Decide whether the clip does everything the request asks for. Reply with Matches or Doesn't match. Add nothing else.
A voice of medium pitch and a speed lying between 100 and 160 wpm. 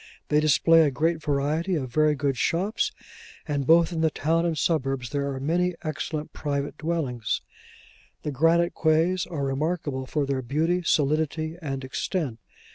Matches